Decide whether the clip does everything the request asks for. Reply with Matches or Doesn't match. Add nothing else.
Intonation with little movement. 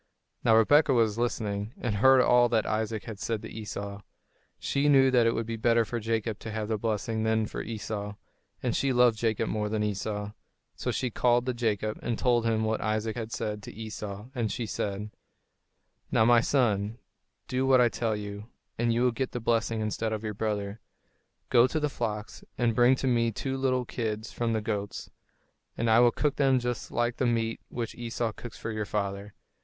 Matches